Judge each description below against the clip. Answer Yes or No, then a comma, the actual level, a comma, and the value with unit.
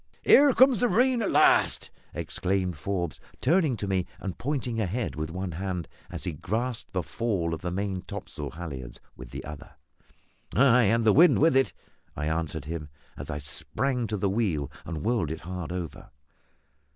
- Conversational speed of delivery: Yes, average, 175 wpm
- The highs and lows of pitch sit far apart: Yes, wide, 6.8 semitones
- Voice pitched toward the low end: Yes, very low, 95 Hz